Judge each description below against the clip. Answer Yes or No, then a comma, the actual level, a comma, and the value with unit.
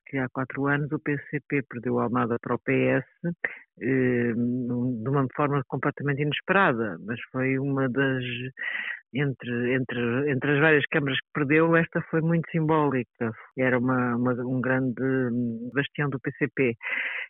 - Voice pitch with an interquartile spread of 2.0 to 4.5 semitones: Yes, average, 2.8 semitones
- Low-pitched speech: Yes, low, 130 Hz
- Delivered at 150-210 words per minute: No, average, 140 wpm